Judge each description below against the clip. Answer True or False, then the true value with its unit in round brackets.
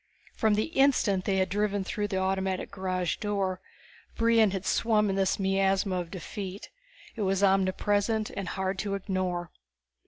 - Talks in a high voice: True (195 Hz)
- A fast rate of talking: False (155 wpm)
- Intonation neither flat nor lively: False (1.6 semitones)